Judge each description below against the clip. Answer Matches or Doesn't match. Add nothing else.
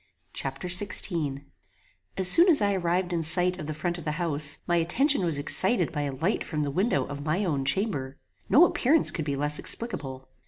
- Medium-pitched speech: Matches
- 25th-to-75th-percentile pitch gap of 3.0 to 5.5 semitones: Matches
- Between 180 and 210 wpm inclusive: Matches